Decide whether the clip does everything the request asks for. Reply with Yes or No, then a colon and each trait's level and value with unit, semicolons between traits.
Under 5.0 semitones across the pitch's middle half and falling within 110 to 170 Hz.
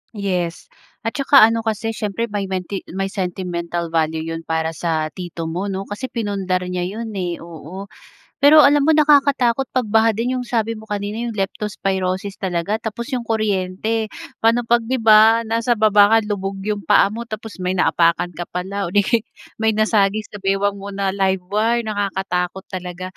No: average, 3.5 semitones; high, 205 Hz